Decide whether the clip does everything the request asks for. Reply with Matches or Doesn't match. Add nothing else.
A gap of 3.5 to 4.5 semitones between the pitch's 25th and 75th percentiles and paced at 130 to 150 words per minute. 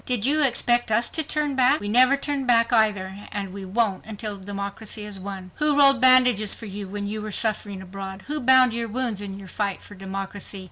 Doesn't match